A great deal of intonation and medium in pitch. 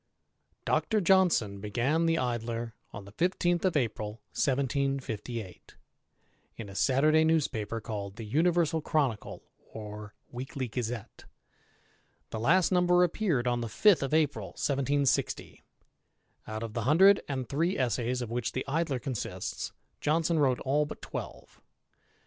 No: wide, 5.8 semitones; low, 130 Hz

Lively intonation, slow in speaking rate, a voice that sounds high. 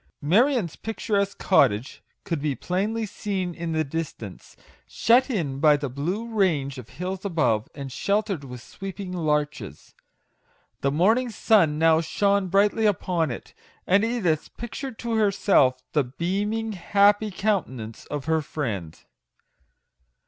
No: wide, 5.9 semitones; slow, 130 wpm; medium, 180 Hz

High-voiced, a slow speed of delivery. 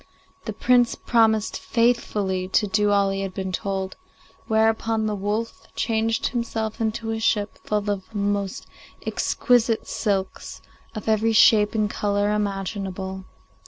Yes: high, 210 Hz; slow, 130 wpm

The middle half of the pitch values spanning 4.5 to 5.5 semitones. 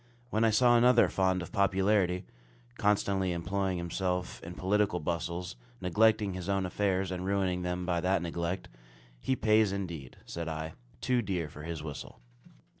No: narrow, 2.5 semitones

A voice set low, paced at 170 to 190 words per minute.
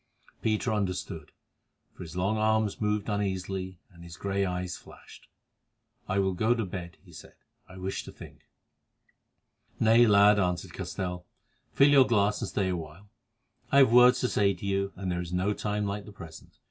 Yes: low, 100 Hz; average, 175 wpm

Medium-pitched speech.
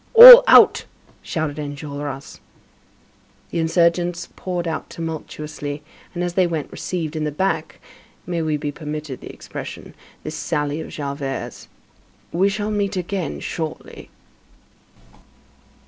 Yes: medium, 160 Hz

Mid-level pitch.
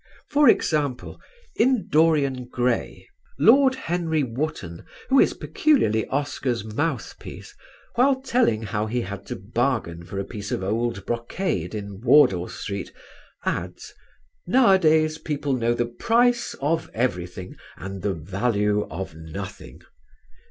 No: low, 120 Hz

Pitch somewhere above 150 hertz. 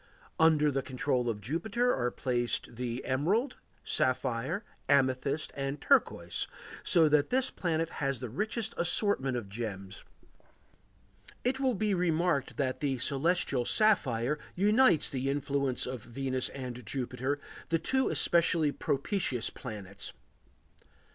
No: medium, 140 Hz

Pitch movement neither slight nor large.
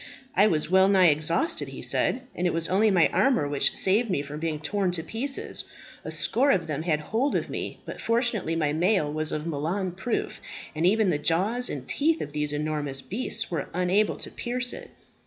No: wide, 6.2 semitones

